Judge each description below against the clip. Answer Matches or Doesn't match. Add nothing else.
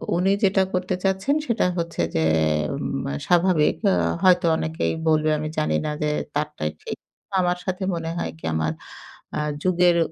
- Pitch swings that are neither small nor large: Matches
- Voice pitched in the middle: Matches